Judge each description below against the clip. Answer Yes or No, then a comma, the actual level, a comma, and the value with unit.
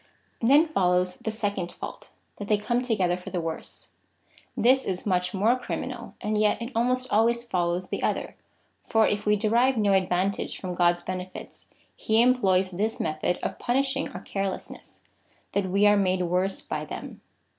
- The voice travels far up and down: No, average, 4.1 semitones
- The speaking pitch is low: No, high, 200 Hz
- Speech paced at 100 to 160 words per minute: No, average, 175 wpm